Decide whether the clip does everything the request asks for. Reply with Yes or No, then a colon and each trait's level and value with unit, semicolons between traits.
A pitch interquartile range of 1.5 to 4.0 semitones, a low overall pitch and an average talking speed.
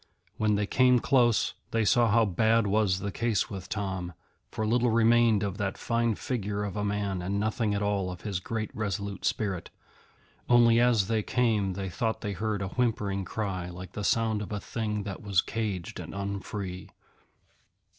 Yes: narrow, 2.5 semitones; low, 105 Hz; average, 180 wpm